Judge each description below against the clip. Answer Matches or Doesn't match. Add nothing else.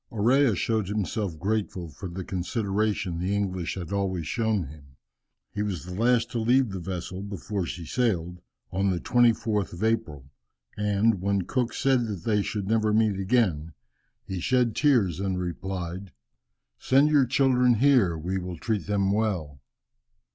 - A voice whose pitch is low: Matches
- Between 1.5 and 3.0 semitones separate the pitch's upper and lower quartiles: Doesn't match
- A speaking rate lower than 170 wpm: Matches